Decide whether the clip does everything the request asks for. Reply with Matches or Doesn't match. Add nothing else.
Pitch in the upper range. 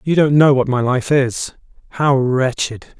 Doesn't match